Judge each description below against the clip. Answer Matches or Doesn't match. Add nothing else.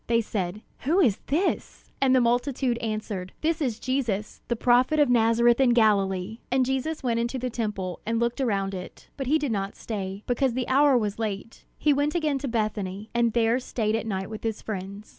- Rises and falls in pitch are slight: Doesn't match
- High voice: Matches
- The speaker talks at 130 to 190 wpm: Doesn't match